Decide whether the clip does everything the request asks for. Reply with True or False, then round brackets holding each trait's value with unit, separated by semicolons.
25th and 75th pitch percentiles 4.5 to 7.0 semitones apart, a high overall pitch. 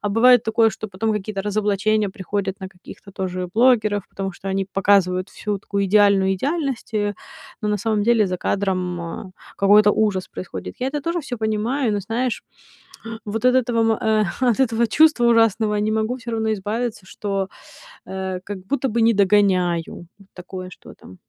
False (2.8 semitones; 210 Hz)